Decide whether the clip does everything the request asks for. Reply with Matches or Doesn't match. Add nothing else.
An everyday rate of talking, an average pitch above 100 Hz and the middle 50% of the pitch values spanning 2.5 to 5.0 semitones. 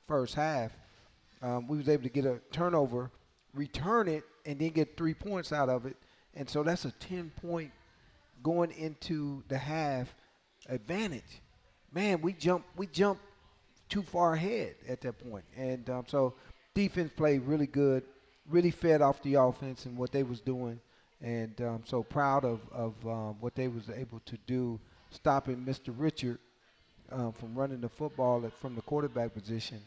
Matches